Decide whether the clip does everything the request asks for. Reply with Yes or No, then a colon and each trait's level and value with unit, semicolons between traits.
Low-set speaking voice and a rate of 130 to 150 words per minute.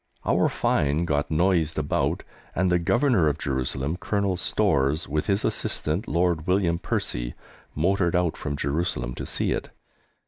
Yes: very low, 85 Hz; average, 145 wpm